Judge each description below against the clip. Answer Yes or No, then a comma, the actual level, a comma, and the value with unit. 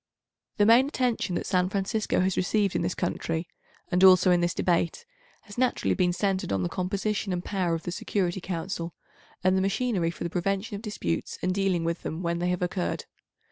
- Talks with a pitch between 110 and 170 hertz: No, medium, 185 Hz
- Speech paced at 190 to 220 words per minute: Yes, average, 200 wpm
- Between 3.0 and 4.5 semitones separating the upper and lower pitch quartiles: No, narrow, 2.4 semitones